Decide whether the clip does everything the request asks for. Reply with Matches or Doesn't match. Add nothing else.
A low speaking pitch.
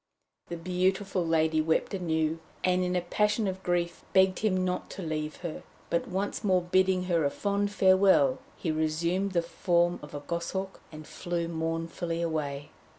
Doesn't match